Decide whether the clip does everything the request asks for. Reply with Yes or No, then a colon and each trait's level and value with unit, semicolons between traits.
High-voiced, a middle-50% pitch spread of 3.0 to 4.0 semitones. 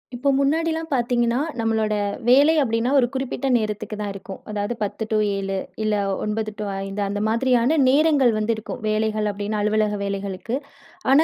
Yes: high, 220 Hz; average, 3.6 semitones